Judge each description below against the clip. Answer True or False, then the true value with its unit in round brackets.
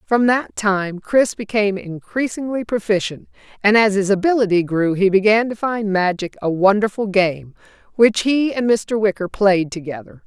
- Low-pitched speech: False (205 Hz)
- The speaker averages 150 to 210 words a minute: True (160 wpm)